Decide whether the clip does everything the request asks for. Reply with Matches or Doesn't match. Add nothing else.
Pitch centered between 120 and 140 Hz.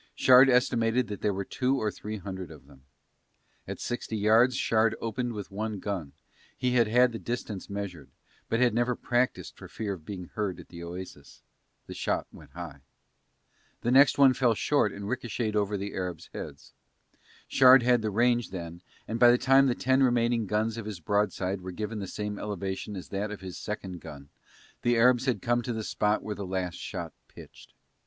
Doesn't match